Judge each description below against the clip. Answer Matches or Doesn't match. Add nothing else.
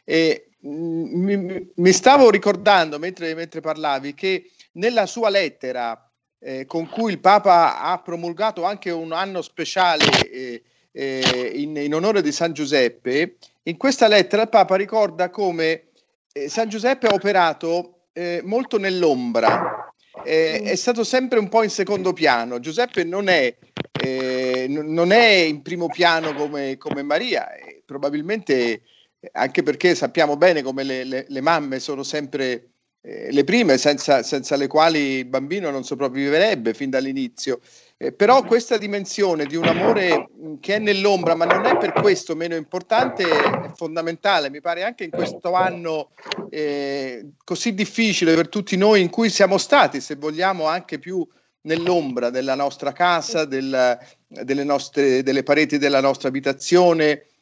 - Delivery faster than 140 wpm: Matches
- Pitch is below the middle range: Doesn't match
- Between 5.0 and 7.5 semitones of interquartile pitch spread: Matches